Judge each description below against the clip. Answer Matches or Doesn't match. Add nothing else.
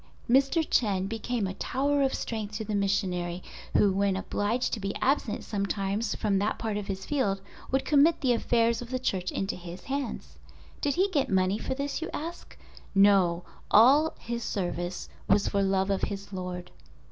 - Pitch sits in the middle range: Doesn't match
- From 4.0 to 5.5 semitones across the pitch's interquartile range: Matches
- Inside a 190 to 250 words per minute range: Doesn't match